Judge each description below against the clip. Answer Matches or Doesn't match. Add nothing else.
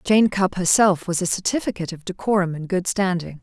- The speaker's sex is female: Matches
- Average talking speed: Matches